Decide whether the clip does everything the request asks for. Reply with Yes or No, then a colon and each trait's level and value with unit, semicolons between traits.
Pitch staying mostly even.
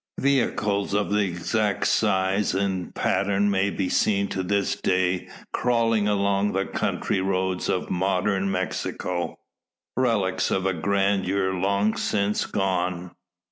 Yes: narrow, 1.5 semitones